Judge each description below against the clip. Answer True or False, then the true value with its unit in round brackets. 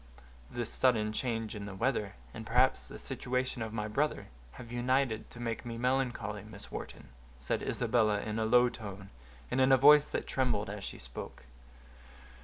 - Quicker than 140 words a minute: True (175 wpm)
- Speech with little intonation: False (3.1 semitones)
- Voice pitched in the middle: False (115 Hz)